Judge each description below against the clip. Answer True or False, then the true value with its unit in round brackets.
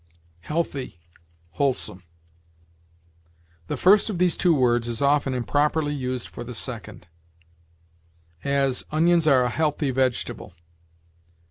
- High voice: False (140 Hz)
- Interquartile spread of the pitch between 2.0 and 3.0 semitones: False (3.8 semitones)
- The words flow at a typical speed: False (110 wpm)